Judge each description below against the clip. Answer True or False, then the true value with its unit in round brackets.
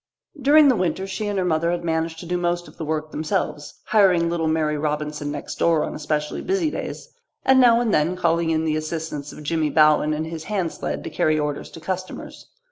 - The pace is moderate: False (215 wpm)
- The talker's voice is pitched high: False (165 Hz)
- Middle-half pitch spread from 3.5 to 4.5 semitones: False (3.1 semitones)